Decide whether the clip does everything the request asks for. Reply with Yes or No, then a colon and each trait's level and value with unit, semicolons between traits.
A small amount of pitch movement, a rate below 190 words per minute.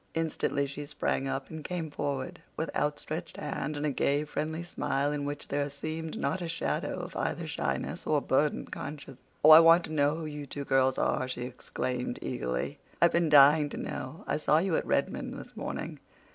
No: narrow, 2.2 semitones; average, 195 wpm